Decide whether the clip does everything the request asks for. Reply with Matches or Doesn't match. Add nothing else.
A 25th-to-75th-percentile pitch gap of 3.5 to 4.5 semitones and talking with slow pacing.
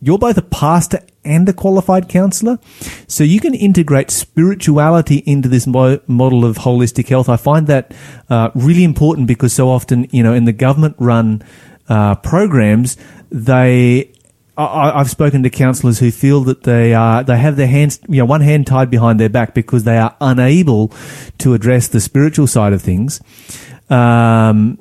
Doesn't match